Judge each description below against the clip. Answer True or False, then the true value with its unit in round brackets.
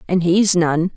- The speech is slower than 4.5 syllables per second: True (3.8 syllables/s)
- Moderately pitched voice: True (175 Hz)